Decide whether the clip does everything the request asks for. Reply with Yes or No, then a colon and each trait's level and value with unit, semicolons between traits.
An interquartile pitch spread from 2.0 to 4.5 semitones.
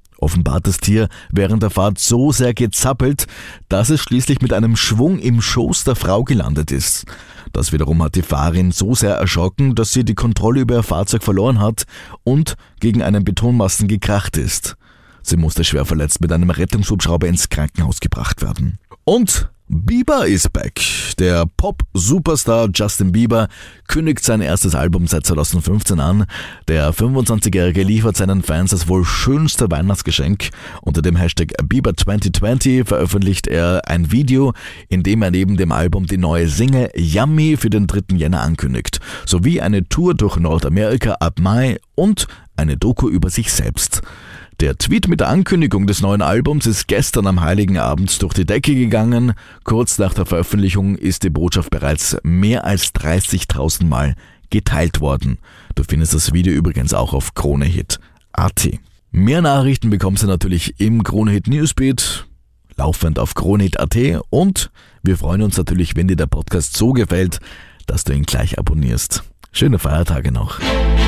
No: average, 5.1 semitones